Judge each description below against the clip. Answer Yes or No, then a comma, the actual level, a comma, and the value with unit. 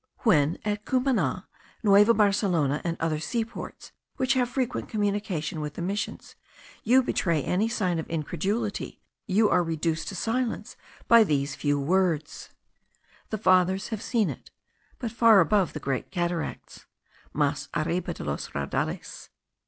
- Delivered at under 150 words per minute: Yes, average, 140 wpm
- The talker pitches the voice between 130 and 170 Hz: No, medium, 185 Hz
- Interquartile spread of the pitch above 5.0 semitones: Yes, wide, 5.6 semitones